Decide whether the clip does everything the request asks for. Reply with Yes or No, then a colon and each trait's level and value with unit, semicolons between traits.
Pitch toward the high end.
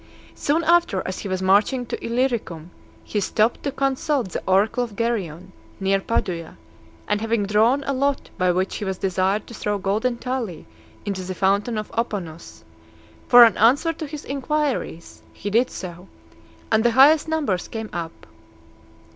Yes: high, 215 Hz